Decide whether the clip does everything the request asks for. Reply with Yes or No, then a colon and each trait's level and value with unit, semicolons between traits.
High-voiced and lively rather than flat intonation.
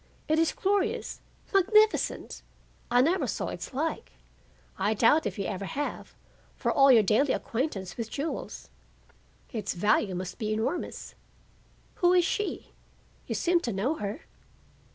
Yes: very high, 270 Hz; wide, 8.3 semitones